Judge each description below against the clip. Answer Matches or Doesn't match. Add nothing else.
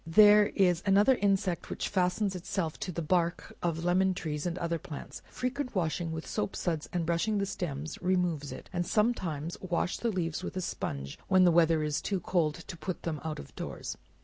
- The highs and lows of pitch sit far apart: Doesn't match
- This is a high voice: Doesn't match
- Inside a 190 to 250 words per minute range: Matches